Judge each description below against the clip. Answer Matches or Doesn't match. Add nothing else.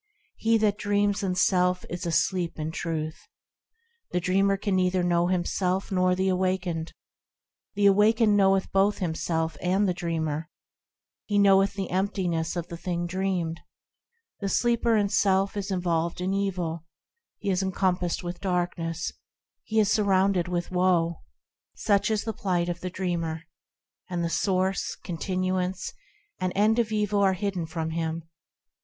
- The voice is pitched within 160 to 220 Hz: Matches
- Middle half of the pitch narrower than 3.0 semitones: Matches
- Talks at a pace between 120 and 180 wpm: Matches